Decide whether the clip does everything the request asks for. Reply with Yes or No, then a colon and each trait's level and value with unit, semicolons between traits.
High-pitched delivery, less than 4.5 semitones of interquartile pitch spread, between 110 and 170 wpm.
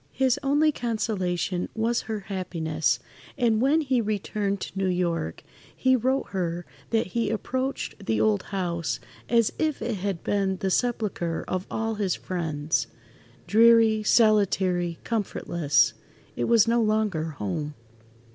No: high, 205 Hz; average, 4.8 semitones; slow, 135 wpm